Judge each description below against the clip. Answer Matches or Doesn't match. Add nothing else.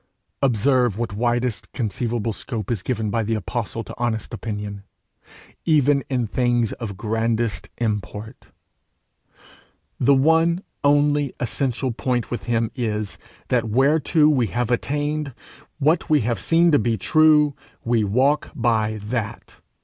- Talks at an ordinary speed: Doesn't match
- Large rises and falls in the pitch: Doesn't match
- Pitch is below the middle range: Matches